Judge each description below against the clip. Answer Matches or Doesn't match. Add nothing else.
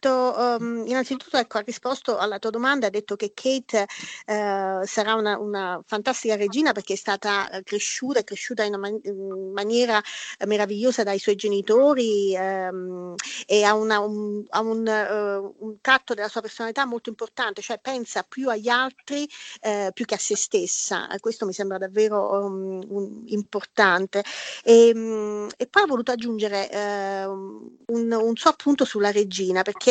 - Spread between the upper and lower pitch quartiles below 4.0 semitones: Matches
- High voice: Matches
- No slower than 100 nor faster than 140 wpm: Doesn't match